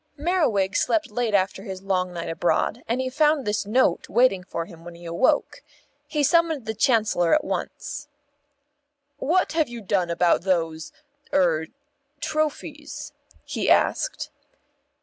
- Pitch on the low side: No, high, 210 Hz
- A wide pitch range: Yes, wide, 8.3 semitones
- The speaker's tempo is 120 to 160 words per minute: Yes, average, 140 wpm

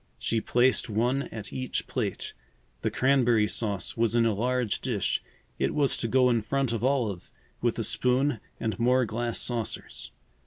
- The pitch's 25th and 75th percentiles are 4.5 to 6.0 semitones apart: No, narrow, 2.5 semitones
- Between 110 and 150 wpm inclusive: No, average, 165 wpm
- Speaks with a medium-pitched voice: No, low, 120 Hz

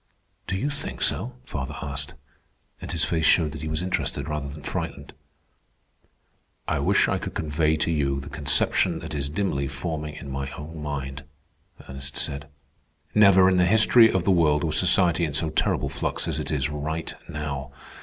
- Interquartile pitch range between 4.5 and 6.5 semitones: No, average, 3.3 semitones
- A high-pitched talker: No, very low, 75 Hz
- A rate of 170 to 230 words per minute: Yes, average, 180 wpm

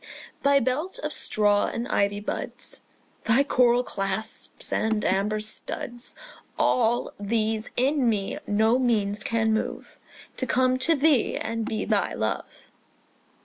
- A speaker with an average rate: No, slow, 130 wpm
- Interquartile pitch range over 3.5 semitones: No, average, 3.1 semitones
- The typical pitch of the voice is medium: No, high, 225 Hz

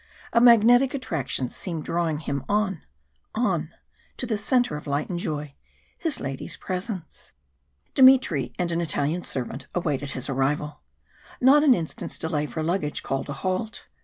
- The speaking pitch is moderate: Yes, medium, 170 Hz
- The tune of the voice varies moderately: No, wide, 7.1 semitones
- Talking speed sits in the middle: Yes, average, 150 wpm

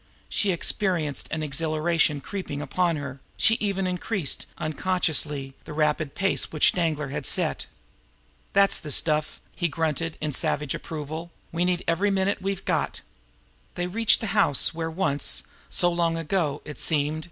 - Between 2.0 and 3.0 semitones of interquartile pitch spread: No, average, 3.5 semitones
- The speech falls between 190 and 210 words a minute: No, average, 155 wpm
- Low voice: No, medium, 165 Hz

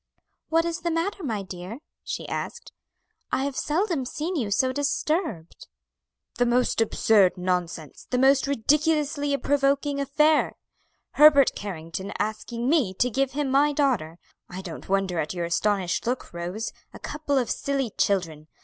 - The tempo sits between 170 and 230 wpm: No, average, 150 wpm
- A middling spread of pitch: No, wide, 7.3 semitones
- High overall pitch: Yes, very high, 255 Hz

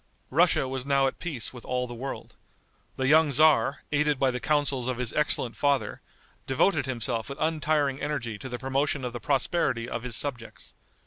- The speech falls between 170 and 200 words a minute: Yes, average, 185 wpm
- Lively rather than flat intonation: No, average, 2.9 semitones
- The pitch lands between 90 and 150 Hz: Yes, low, 135 Hz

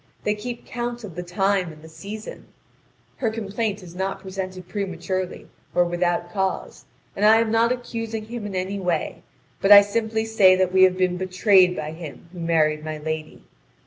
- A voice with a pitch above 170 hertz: Yes, high, 190 Hz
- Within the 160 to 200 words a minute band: Yes, average, 180 wpm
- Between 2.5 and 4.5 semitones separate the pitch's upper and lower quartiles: Yes, average, 3.6 semitones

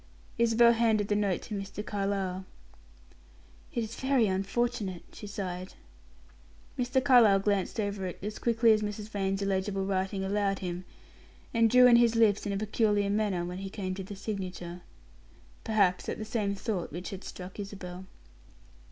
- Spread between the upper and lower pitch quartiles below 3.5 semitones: Yes, narrow, 2.4 semitones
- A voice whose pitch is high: Yes, high, 200 Hz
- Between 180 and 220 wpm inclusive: No, average, 160 wpm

